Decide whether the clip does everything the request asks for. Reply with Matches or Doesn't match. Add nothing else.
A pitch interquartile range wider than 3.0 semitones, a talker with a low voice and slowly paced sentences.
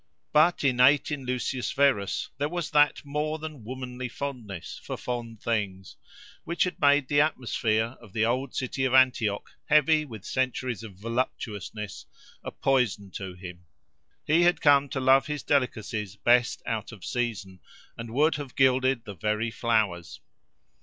Doesn't match